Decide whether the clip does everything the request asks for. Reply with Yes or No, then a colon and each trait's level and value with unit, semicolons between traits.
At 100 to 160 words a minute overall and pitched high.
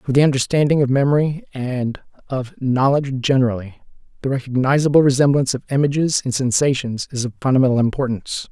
No: average, 140 wpm; low, 135 Hz